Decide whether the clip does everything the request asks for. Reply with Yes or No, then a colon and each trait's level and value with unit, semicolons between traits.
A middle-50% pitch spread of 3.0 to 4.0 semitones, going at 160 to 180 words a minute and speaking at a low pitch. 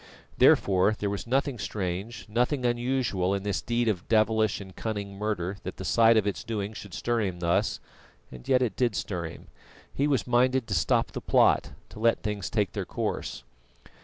No: average, 3.6 semitones; average, 190 wpm; low, 105 Hz